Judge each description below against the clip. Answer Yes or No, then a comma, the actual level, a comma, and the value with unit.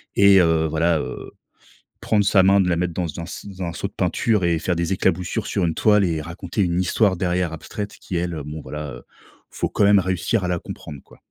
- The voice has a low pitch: Yes, very low, 90 Hz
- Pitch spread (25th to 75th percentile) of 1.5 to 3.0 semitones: Yes, average, 2.7 semitones